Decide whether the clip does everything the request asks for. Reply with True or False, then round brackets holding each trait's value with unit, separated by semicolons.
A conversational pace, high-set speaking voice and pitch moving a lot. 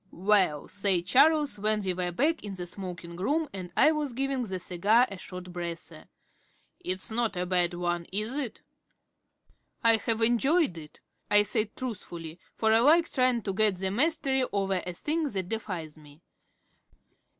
True (165 wpm; 200 Hz; 5.7 semitones)